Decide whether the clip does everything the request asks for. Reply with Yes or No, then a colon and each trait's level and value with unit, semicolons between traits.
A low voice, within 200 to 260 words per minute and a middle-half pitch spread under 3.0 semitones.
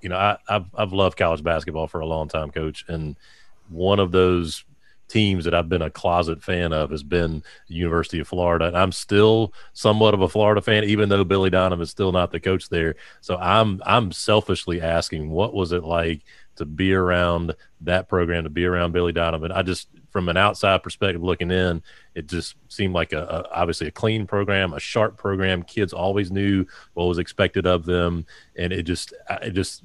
Yes: very low, 90 Hz; fast, 205 wpm; narrow, 2.6 semitones